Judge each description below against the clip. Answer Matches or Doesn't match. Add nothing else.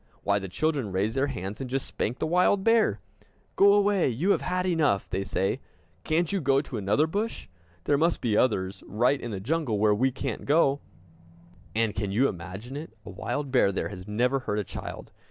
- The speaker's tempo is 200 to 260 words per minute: Matches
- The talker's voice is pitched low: Matches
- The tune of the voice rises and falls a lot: Matches